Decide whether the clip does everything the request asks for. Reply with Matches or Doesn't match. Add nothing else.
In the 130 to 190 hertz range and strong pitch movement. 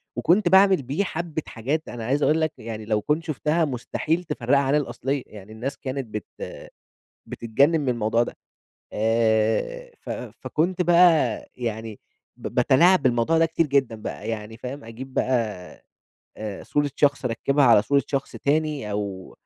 Matches